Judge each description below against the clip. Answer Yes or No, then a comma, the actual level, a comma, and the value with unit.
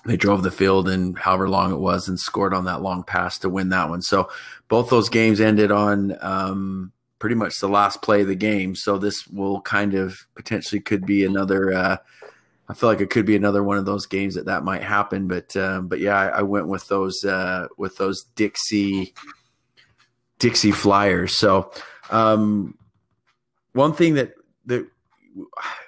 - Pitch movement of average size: No, narrow, 2.1 semitones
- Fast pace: No, average, 185 wpm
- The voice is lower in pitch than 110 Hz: Yes, low, 100 Hz